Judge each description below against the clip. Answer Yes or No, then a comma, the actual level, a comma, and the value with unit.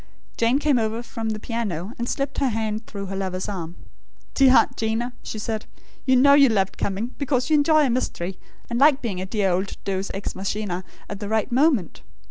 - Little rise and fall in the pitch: No, average, 4.6 semitones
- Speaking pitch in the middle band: No, high, 220 Hz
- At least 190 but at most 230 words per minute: Yes, fast, 205 wpm